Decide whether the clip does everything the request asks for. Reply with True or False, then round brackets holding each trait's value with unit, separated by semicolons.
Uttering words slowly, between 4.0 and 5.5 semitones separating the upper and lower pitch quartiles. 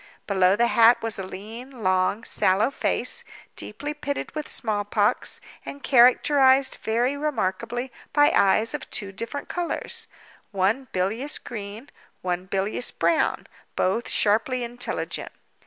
True (125 wpm; 4.9 semitones)